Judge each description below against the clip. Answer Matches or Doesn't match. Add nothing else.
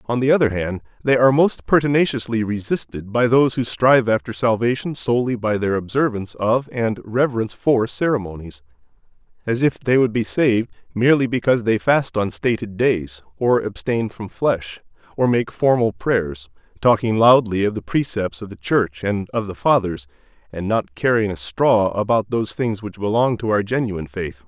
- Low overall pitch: Matches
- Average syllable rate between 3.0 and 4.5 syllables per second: Doesn't match